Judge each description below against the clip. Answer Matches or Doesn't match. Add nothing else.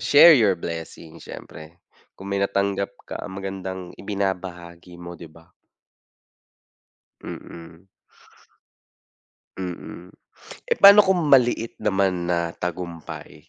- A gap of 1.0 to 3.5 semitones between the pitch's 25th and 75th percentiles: Matches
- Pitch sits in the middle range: Doesn't match